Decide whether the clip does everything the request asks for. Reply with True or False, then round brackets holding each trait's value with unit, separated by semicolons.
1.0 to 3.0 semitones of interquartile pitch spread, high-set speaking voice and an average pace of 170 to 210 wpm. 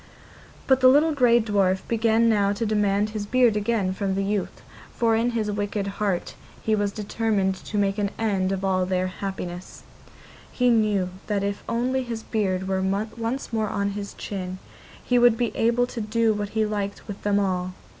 True (2.6 semitones; 210 Hz; 185 wpm)